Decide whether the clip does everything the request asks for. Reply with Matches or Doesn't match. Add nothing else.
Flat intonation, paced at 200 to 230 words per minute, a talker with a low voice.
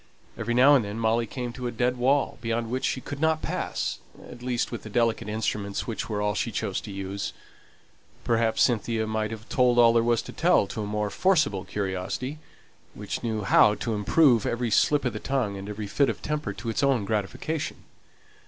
Doesn't match